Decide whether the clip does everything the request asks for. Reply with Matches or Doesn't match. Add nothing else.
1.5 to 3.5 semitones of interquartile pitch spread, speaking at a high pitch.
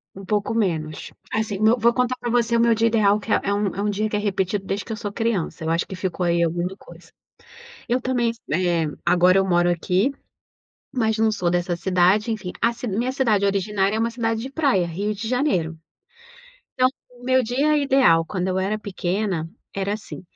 Doesn't match